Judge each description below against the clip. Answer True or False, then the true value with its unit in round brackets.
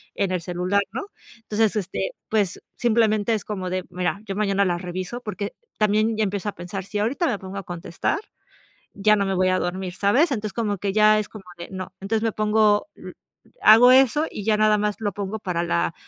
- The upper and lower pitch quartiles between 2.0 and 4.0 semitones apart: True (2.5 semitones)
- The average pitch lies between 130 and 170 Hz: False (205 Hz)